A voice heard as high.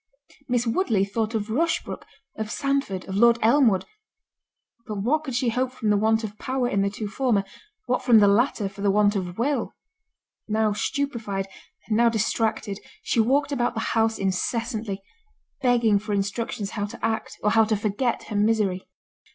Yes: high, 220 Hz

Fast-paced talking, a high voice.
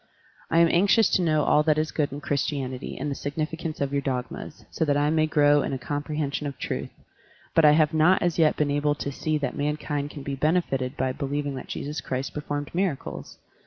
No: fast, 220 wpm; medium, 145 Hz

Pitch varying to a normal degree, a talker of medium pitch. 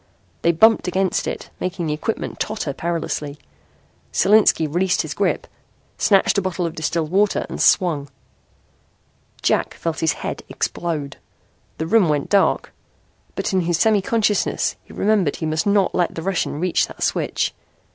Yes: average, 3.7 semitones; medium, 175 Hz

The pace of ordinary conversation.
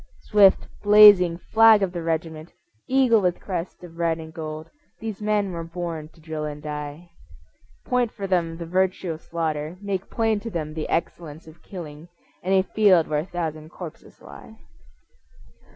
Yes: average, 170 wpm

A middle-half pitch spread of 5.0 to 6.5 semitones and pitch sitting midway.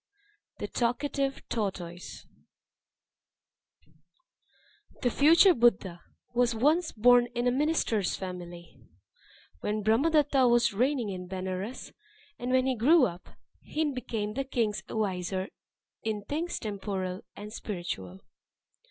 No: wide, 5.6 semitones; high, 225 Hz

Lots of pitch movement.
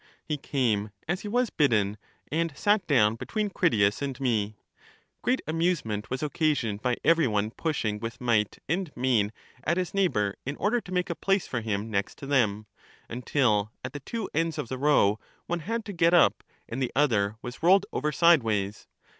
Yes: wide, 7.7 semitones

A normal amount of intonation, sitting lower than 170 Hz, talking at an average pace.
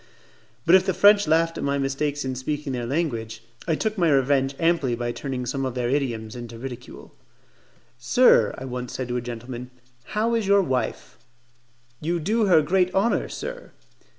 No: wide, 5.8 semitones; medium, 140 Hz; average, 180 wpm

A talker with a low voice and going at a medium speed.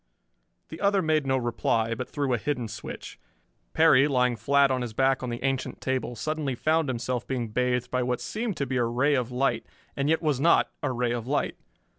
No: low, 130 Hz; fast, 210 wpm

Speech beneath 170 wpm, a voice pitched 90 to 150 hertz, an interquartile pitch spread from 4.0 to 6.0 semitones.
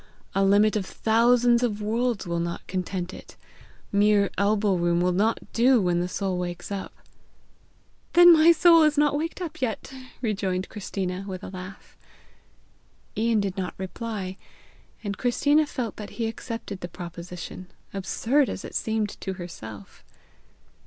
No: average, 150 wpm; high, 205 Hz; average, 4.3 semitones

